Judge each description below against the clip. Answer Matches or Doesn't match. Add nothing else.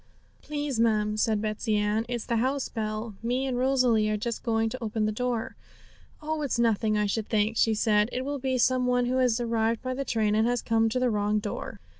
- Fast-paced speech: Matches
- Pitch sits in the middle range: Doesn't match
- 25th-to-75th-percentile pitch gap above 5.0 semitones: Doesn't match